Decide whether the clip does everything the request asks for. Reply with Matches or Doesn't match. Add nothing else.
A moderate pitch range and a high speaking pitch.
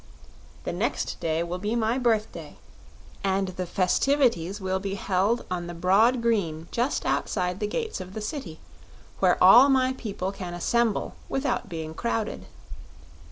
Matches